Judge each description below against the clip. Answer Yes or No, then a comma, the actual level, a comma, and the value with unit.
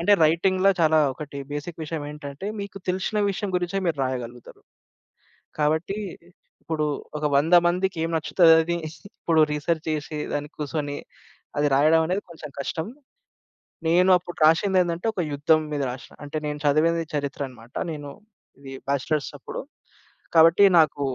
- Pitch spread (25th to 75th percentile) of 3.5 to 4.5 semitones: No, average, 2.8 semitones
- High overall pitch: No, medium, 160 Hz